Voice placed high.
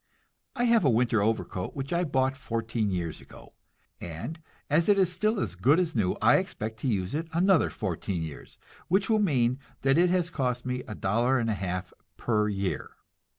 No: low, 125 Hz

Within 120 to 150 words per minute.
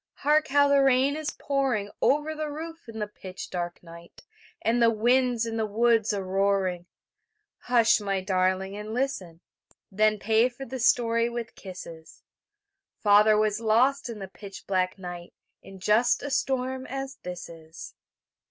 No: average, 160 wpm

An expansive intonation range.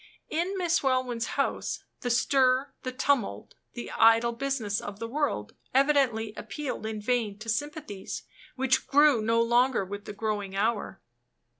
No: average, 3.9 semitones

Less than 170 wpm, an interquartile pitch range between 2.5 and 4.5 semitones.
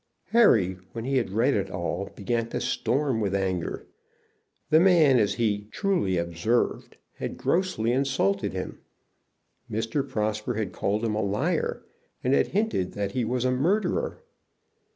No: average, 150 wpm; average, 5.2 semitones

